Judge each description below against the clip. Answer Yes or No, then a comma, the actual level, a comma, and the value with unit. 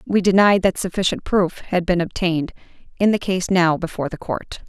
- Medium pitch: Yes, medium, 180 Hz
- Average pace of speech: Yes, average, 190 wpm